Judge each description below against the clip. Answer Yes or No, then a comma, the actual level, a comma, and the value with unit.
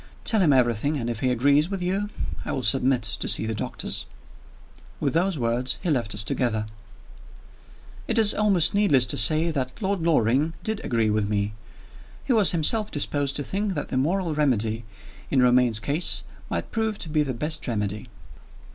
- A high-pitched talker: No, medium, 140 Hz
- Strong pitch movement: Yes, wide, 6.9 semitones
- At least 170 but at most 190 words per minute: Yes, average, 180 wpm